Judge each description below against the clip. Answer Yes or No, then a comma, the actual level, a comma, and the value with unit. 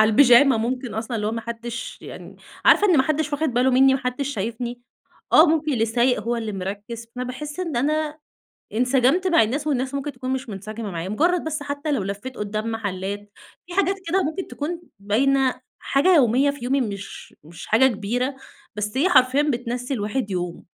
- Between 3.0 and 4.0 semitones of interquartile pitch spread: No, average, 4.5 semitones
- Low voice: No, very high, 250 Hz